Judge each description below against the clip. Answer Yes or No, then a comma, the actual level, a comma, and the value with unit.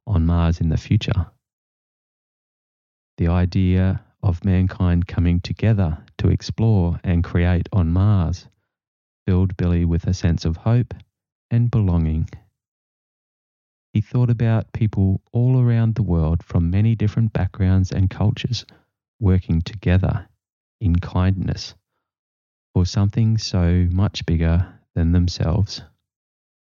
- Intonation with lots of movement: No, average, 3.9 semitones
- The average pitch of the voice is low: Yes, very low, 95 Hz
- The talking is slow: Yes, slow, 115 wpm